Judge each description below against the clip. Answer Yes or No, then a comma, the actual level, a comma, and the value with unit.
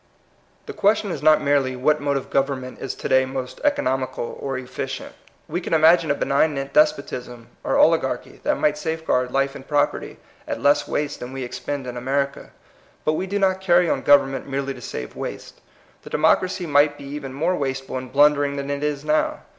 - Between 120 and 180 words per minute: No, average, 195 wpm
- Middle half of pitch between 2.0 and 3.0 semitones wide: Yes, narrow, 2.4 semitones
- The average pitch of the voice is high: No, medium, 140 Hz